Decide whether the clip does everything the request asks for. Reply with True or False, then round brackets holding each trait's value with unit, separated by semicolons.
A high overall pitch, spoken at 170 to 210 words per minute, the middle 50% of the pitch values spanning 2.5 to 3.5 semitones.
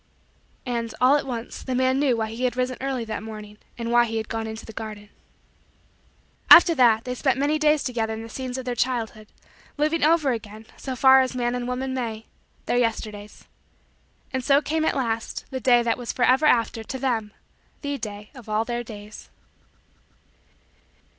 True (245 Hz; 185 wpm; 2.8 semitones)